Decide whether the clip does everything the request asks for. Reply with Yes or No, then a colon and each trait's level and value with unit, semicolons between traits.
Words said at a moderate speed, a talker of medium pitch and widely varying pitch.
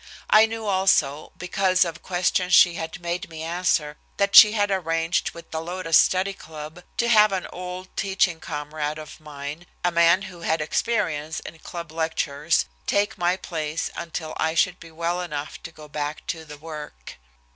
No: average, 175 wpm; medium, 170 Hz; average, 2.9 semitones